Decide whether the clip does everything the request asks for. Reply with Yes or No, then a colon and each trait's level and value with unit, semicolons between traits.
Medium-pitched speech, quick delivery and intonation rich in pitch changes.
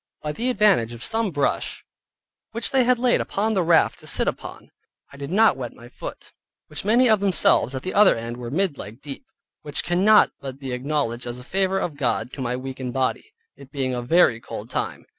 Yes: medium, 145 Hz; fast, 215 wpm; wide, 8.0 semitones